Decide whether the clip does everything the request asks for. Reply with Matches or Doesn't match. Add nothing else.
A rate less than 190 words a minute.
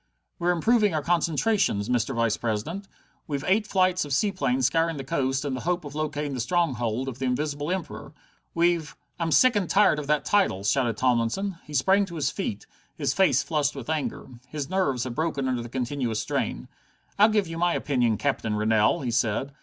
Doesn't match